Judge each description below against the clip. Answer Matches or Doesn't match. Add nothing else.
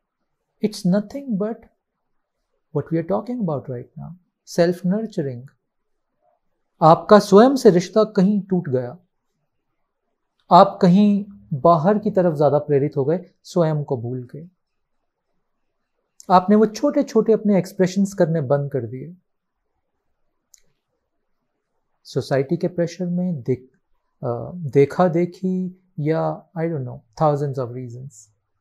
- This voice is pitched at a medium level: Matches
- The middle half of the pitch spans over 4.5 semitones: Matches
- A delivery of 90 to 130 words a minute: Matches